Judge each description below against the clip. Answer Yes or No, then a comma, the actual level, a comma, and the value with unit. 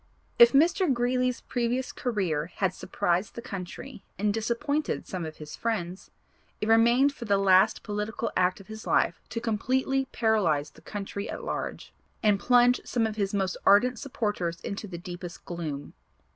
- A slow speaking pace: No, average, 160 wpm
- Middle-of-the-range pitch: No, high, 210 Hz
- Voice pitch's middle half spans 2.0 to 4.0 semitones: No, average, 4.7 semitones